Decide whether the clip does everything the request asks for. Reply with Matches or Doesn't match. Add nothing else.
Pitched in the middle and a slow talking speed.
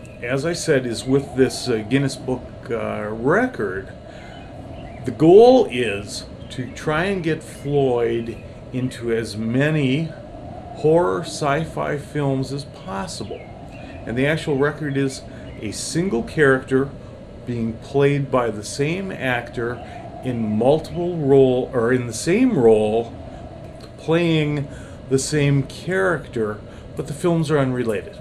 Doesn't match